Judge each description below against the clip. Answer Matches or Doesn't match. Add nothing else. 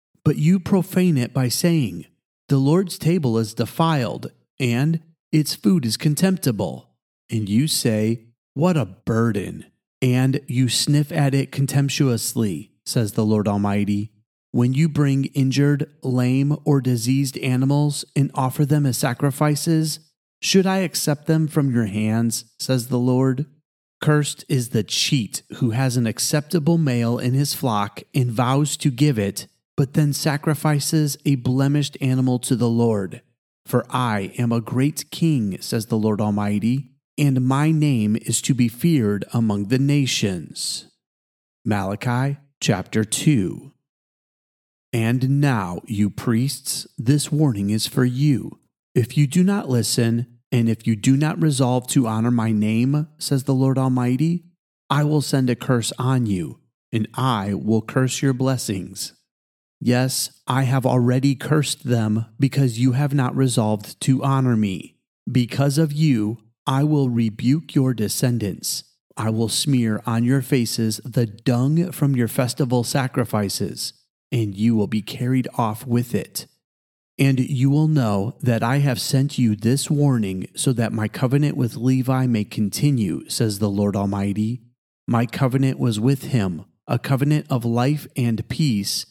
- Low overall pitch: Matches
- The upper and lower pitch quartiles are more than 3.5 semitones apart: Matches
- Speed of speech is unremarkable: Matches